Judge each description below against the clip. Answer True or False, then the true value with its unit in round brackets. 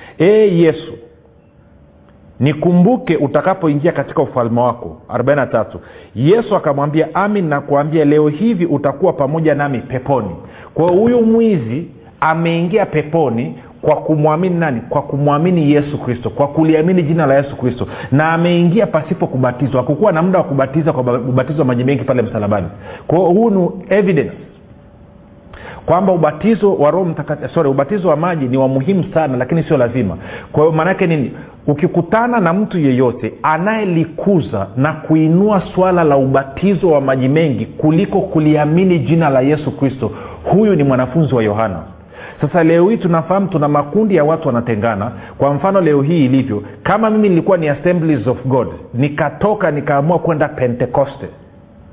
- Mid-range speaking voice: True (155 Hz)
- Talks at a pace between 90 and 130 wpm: False (140 wpm)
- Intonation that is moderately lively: True (4.9 semitones)